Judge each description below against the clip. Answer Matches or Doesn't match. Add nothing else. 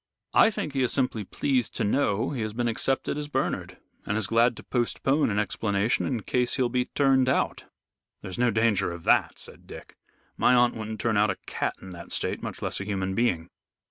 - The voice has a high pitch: Doesn't match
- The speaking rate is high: Matches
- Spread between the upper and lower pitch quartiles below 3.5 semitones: Doesn't match